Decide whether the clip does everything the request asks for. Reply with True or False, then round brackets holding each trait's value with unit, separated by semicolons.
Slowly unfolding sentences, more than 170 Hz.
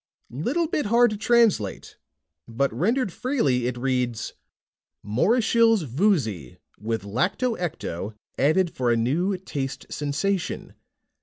False (110 wpm; 150 Hz)